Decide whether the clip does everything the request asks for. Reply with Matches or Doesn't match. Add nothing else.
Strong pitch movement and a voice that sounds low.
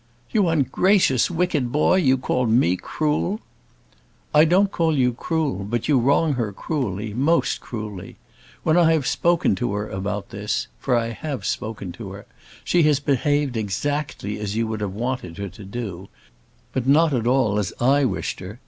Matches